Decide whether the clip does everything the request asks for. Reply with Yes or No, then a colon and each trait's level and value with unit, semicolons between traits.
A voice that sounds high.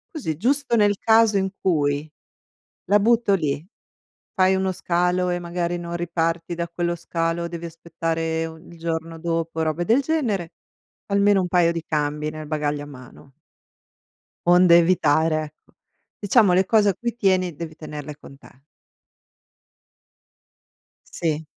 No: medium, 170 Hz